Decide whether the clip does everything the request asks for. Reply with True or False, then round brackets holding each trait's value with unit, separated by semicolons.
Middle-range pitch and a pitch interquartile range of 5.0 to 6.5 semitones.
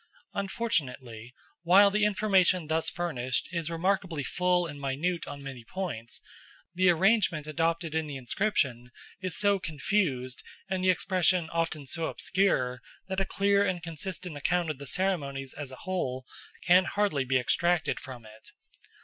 True (165 Hz; 5.4 semitones)